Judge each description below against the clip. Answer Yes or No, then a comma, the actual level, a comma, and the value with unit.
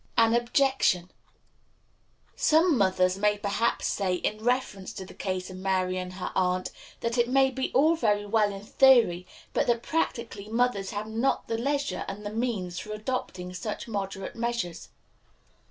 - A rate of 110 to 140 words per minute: No, average, 160 wpm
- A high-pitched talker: Yes, high, 215 Hz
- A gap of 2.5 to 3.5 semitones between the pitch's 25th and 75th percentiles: No, average, 4.1 semitones